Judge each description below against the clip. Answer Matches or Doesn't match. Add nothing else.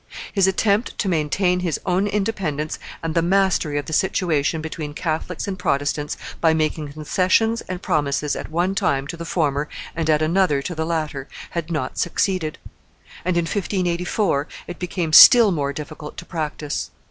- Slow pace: Doesn't match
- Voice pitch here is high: Doesn't match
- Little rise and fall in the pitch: Doesn't match